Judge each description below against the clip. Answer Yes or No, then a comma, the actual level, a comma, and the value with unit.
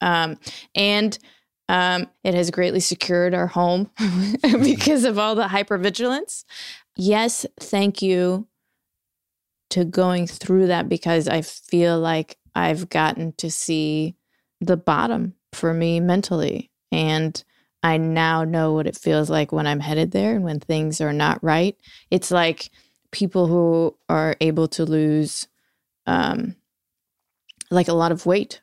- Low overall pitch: No, medium, 175 Hz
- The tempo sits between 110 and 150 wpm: Yes, average, 140 wpm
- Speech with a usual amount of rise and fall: Yes, average, 3.5 semitones